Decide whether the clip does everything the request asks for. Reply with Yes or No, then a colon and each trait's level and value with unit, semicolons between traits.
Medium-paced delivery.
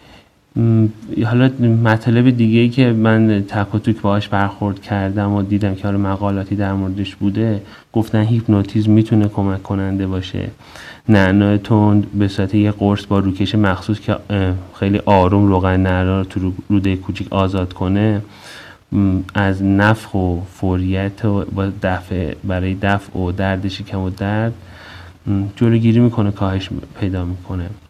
Yes: average, 130 wpm